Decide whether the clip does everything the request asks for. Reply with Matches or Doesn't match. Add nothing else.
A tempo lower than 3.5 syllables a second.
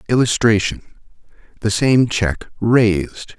Doesn't match